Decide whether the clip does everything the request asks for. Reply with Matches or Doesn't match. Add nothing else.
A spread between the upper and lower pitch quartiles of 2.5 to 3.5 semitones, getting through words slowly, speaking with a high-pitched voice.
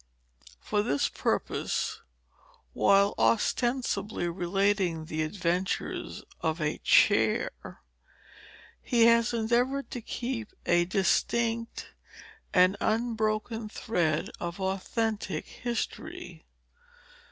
Doesn't match